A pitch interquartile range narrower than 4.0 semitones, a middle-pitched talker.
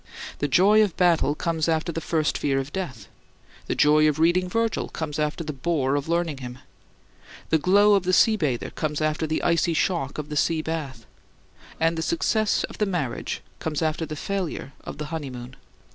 Yes: average, 2.9 semitones; medium, 160 Hz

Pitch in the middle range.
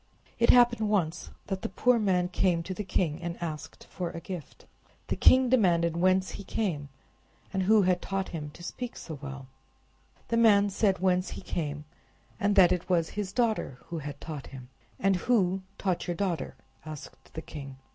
Yes: medium, 180 Hz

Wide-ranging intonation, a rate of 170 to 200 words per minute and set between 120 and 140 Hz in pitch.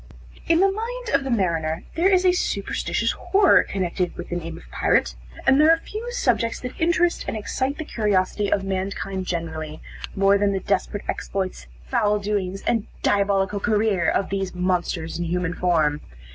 No: wide, 6.4 semitones; average, 175 wpm; high, 195 Hz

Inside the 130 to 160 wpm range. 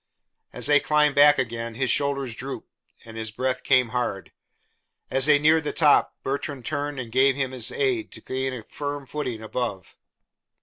No: average, 175 wpm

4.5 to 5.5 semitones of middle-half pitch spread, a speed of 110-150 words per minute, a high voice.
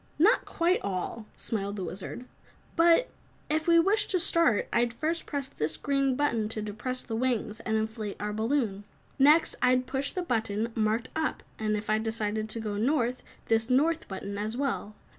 No: average, 5.0 semitones; average, 180 wpm; high, 230 Hz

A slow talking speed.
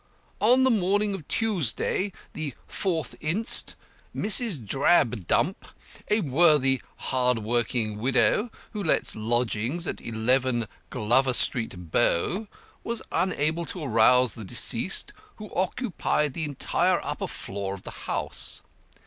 Yes: slow, 120 wpm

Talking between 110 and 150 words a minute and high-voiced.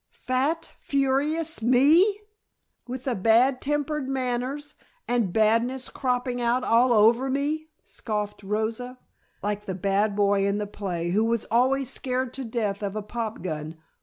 Yes: average, 145 wpm; high, 245 Hz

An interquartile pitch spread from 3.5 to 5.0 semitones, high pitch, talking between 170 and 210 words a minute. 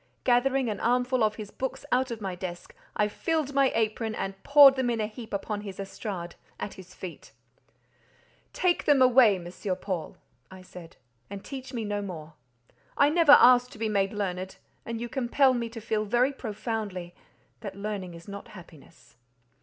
Yes: average, 4.5 semitones; high, 215 Hz; average, 175 wpm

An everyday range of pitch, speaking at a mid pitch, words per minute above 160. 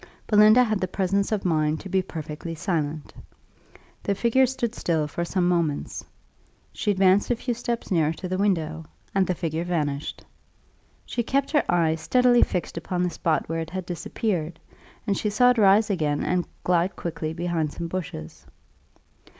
Yes: average, 4.2 semitones; medium, 180 Hz; average, 170 wpm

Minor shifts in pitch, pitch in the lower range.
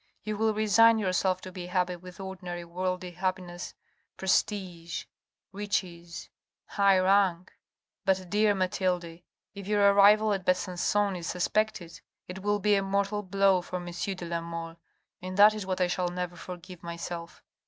No: narrow, 2.3 semitones; medium, 185 Hz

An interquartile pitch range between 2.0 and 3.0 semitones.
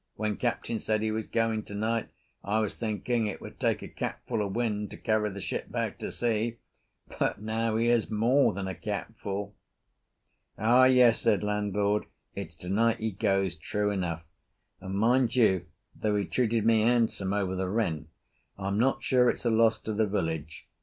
Yes: narrow, 2.4 semitones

